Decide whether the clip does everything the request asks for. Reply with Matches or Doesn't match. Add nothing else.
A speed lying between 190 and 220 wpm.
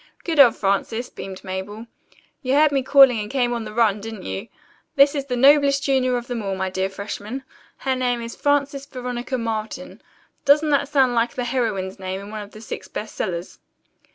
Matches